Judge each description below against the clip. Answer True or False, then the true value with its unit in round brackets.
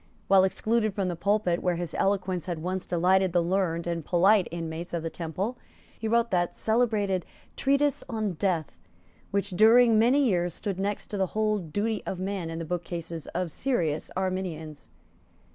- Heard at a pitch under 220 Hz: True (185 Hz)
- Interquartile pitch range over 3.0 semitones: True (3.8 semitones)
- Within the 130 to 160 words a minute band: False (170 wpm)